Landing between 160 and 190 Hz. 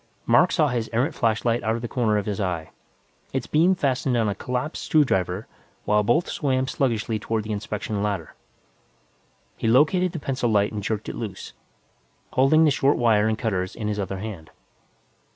No: low, 115 Hz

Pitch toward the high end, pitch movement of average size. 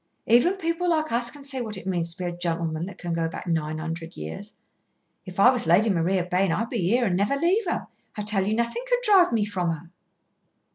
No: high, 195 Hz; wide, 6.3 semitones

